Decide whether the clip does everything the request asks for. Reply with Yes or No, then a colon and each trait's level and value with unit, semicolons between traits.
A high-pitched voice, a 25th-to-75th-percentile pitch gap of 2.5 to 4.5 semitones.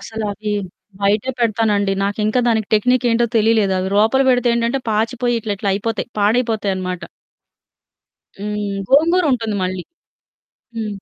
Yes: high, 220 Hz; average, 2.8 semitones